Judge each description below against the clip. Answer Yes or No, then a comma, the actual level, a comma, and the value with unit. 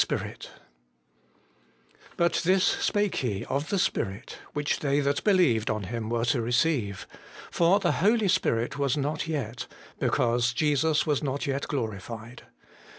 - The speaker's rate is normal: Yes, average, 145 wpm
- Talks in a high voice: No, medium, 140 Hz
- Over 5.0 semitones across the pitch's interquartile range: Yes, wide, 5.4 semitones